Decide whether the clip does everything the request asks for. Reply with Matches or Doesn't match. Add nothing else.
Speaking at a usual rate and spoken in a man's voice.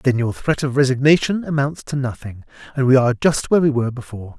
Doesn't match